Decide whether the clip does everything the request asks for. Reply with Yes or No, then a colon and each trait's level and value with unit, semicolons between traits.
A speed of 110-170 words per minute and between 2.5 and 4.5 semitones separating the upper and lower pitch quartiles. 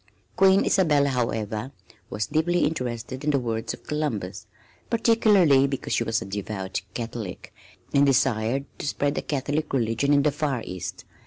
No: average, 155 wpm; average, 4.9 semitones